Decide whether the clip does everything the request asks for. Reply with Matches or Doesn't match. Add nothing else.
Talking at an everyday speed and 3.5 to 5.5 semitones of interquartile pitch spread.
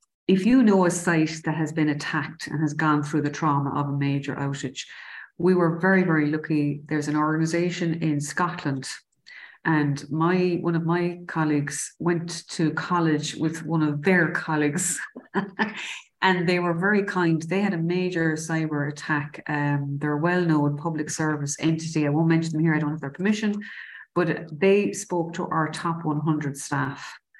Doesn't match